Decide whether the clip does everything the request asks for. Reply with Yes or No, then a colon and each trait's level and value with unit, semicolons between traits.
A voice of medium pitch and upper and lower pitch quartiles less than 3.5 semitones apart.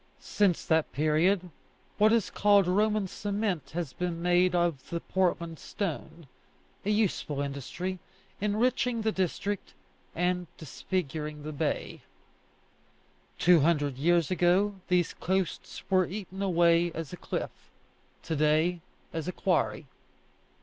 Yes: medium, 175 Hz; average, 3.1 semitones